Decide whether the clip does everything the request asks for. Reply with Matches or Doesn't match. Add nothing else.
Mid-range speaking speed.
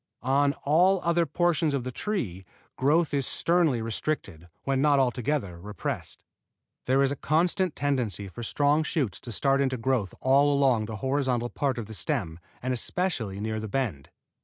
Matches